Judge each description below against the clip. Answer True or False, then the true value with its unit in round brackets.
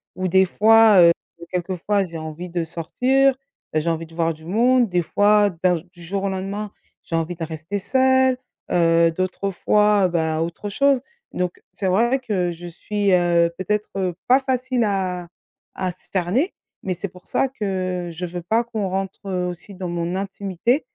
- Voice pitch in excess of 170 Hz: True (185 Hz)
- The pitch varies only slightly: False (3.4 semitones)